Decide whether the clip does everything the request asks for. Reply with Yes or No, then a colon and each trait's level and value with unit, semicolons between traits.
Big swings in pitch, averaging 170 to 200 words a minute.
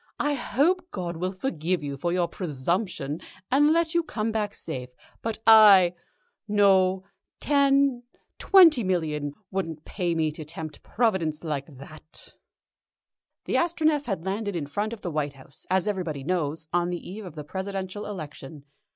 No: wide, 5.8 semitones; average, 155 wpm